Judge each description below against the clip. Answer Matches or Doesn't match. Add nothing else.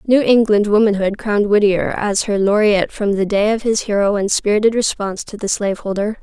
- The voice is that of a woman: Matches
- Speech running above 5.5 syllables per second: Matches